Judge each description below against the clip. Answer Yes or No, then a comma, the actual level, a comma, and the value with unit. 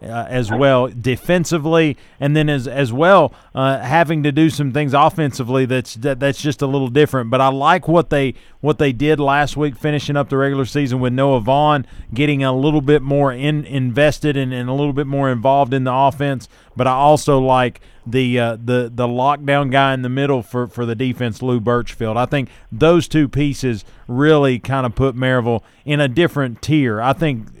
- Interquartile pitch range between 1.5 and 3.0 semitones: Yes, narrow, 2.6 semitones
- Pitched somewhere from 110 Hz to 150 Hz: Yes, low, 135 Hz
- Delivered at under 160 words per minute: No, average, 200 wpm